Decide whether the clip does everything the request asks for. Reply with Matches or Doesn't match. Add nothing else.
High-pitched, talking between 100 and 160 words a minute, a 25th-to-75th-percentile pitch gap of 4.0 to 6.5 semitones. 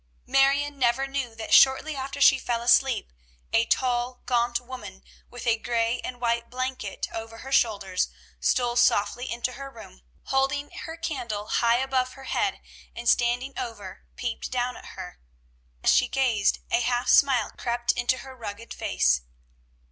Doesn't match